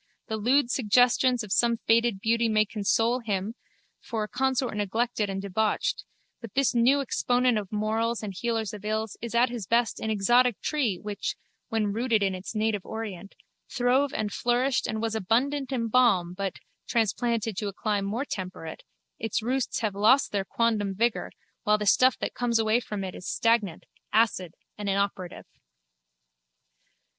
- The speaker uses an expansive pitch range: No, average, 2.8 semitones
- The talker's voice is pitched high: Yes, high, 225 Hz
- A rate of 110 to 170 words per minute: Yes, average, 165 wpm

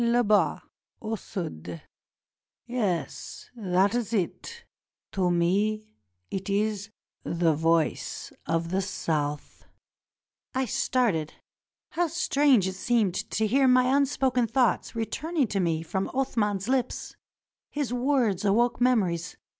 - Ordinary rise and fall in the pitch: No, wide, 5.8 semitones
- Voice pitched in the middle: No, high, 215 Hz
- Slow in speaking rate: Yes, slow, 115 wpm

